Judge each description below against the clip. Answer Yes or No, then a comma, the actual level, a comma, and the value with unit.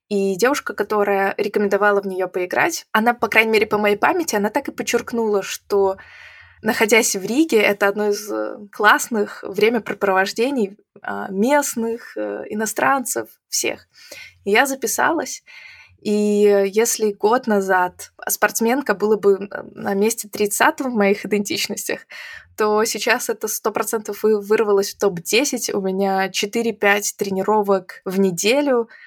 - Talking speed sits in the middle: Yes, average, 120 wpm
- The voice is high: Yes, high, 210 Hz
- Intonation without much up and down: Yes, narrow, 2.2 semitones